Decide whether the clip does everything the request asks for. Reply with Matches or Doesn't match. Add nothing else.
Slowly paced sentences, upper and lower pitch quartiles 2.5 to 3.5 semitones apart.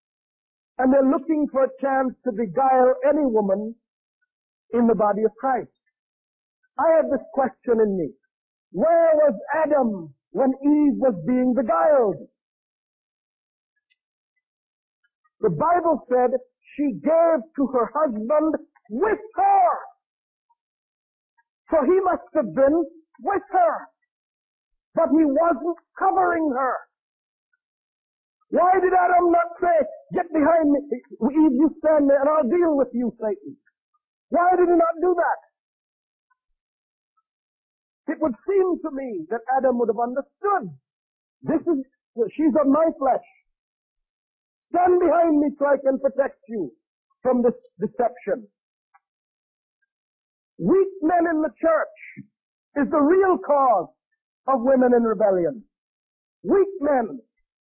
Doesn't match